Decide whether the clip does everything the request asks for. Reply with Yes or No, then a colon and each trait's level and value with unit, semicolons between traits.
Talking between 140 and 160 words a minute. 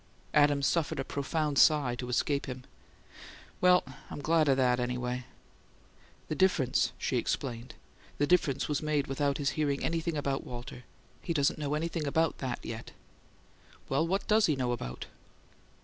Yes: average, 150 wpm